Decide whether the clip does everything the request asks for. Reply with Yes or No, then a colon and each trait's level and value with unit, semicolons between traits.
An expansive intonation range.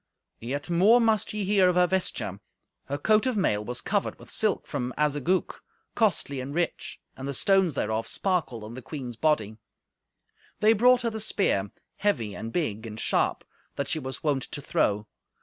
Yes: wide, 8.6 semitones